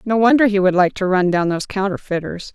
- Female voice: Yes, female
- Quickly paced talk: Yes, fast, 235 wpm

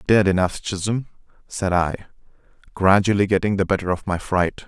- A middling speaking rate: Yes, average, 155 wpm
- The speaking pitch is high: No, very low, 95 Hz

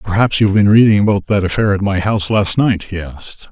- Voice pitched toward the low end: Yes, low, 100 Hz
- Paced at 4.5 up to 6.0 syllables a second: No, 6.2 syllables/s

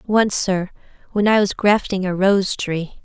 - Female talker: Yes, female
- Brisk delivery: No, average, 180 wpm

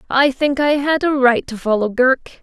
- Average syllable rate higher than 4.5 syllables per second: Yes, 5.0 syllables/s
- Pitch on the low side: No, very high, 265 Hz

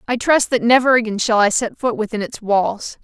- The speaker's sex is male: No, female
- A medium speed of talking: No, fast, 235 wpm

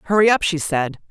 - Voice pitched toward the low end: No, medium, 175 Hz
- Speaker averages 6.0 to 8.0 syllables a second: Yes, 6.3 syllables/s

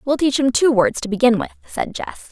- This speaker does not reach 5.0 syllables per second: No, 5.3 syllables/s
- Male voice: No, female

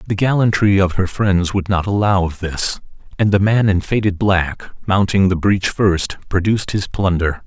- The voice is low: Yes, very low, 95 Hz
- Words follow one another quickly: No, average, 195 wpm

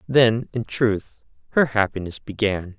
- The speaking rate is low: Yes, slow, 130 wpm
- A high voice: No, low, 110 Hz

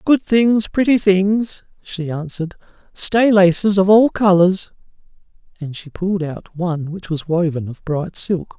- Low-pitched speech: No, medium, 185 Hz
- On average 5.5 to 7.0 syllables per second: No, 4.3 syllables/s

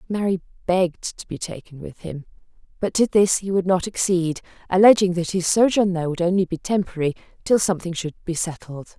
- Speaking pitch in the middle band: Yes, medium, 180 Hz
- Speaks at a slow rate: No, average, 185 wpm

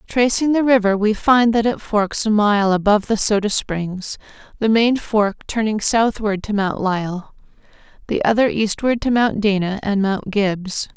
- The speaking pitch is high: Yes, high, 210 Hz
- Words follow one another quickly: No, average, 170 wpm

